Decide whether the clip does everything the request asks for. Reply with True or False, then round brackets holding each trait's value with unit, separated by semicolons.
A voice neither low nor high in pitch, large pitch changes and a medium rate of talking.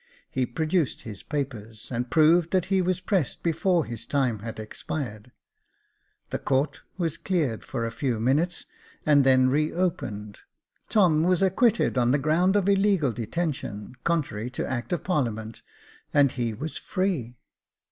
True (145 Hz; 6.6 semitones; 150 wpm)